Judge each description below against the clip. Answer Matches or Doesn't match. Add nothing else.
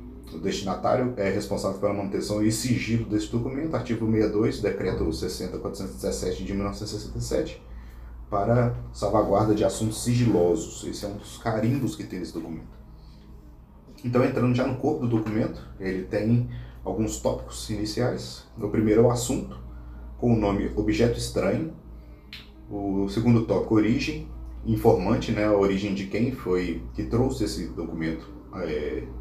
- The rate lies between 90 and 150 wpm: Matches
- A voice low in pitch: Matches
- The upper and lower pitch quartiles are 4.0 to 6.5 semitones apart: Matches